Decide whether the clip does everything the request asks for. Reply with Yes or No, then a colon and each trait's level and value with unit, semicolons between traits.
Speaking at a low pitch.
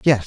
Yes: low, 125 Hz